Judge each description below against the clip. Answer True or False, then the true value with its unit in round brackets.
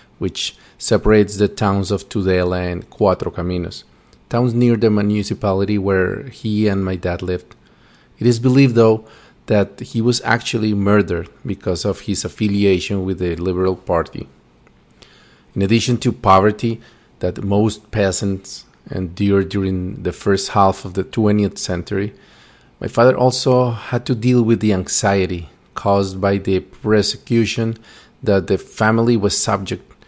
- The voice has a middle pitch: False (100 Hz)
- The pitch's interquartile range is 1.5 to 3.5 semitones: True (3.2 semitones)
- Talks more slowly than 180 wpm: True (140 wpm)